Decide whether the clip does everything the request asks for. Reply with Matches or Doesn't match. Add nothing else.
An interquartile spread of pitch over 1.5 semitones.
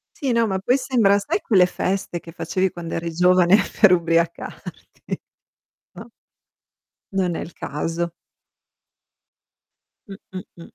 Matches